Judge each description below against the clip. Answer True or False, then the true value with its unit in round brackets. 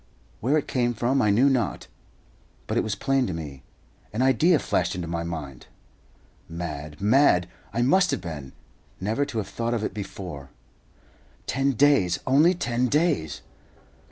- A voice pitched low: True (115 Hz)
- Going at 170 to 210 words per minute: False (155 wpm)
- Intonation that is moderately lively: False (8.0 semitones)